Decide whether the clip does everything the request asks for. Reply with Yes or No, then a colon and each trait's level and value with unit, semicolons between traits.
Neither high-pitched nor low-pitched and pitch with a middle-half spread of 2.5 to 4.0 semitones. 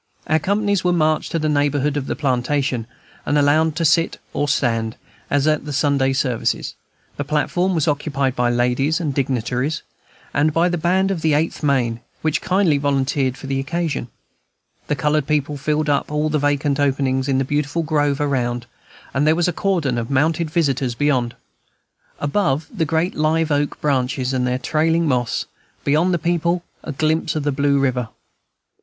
Yes: medium, 145 Hz; average, 2.9 semitones